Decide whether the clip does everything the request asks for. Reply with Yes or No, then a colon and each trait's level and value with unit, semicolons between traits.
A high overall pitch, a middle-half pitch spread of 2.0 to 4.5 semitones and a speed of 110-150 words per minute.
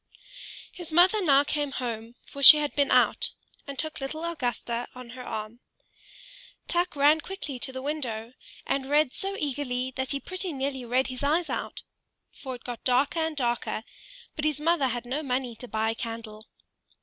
No: very high, 270 Hz; average, 3.7 semitones; average, 180 wpm